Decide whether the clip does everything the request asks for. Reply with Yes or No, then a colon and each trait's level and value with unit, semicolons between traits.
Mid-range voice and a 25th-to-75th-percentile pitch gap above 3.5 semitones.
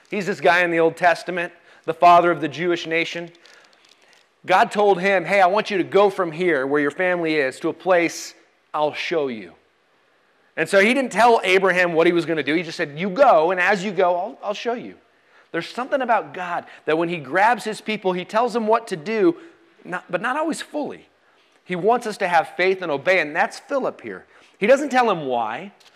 Yes: medium, 180 Hz; average, 4.1 semitones